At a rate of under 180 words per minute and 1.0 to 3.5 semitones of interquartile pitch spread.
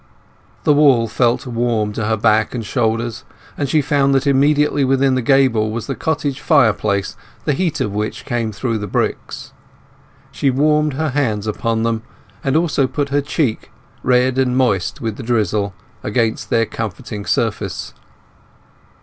No: average, 150 wpm; average, 4.0 semitones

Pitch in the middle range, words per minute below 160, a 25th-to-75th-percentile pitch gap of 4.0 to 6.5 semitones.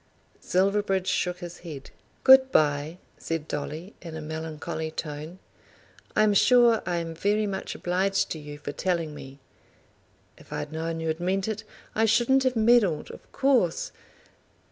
Yes: medium, 175 Hz; average, 150 wpm; average, 4.8 semitones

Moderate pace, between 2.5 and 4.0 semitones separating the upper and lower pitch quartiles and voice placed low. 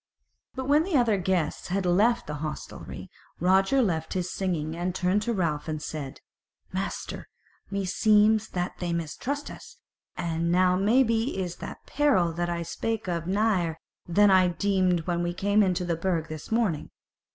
No: average, 165 wpm; average, 3.6 semitones; medium, 185 Hz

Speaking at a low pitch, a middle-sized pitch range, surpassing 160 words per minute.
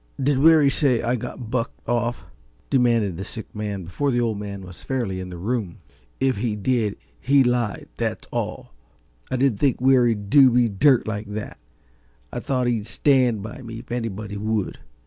Yes: low, 115 Hz; average, 3.7 semitones; average, 180 wpm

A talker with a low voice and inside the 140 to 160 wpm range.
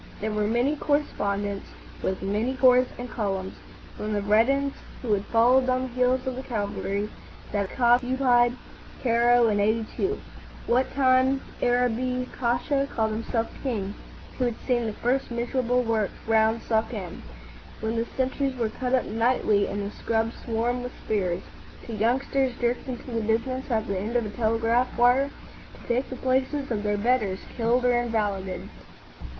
No: high, 235 Hz; average, 155 wpm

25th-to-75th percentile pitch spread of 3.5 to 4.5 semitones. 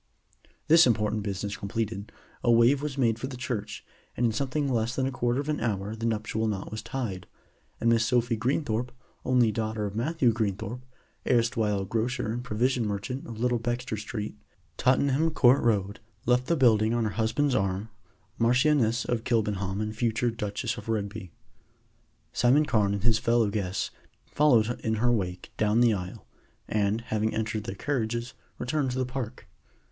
No: average, 2.7 semitones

